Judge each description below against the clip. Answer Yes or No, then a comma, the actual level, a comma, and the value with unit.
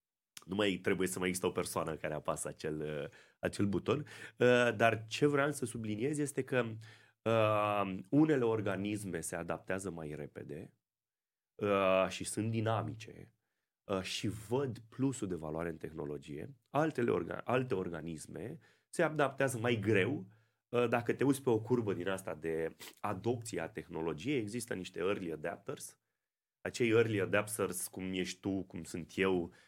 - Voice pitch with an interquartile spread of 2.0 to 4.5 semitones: No, average, 5.0 semitones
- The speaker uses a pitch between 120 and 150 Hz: No, low, 105 Hz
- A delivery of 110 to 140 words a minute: Yes, average, 135 wpm